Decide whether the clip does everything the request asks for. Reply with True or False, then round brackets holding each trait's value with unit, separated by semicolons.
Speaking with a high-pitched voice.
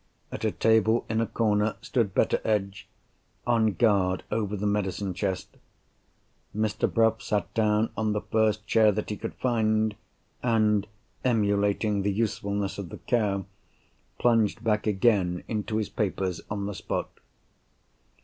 False (105 Hz)